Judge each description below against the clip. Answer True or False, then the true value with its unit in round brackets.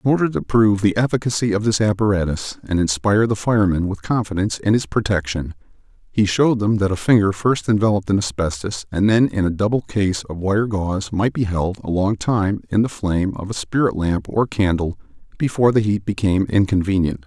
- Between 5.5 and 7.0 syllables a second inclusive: True (5.9 syllables/s)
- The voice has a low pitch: True (100 Hz)